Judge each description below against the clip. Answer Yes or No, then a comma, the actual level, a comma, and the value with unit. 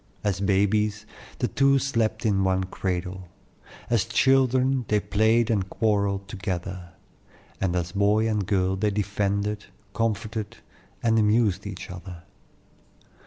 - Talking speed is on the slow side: Yes, slow, 120 wpm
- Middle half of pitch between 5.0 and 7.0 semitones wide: No, average, 2.7 semitones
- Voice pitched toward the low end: Yes, low, 105 Hz